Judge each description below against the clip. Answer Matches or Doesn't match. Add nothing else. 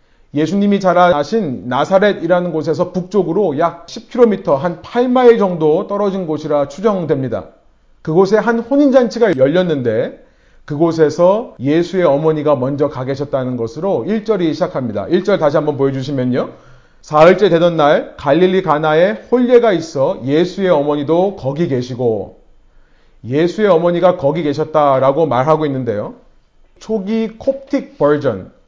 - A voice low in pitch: Doesn't match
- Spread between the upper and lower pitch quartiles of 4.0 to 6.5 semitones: Matches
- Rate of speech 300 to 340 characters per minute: Matches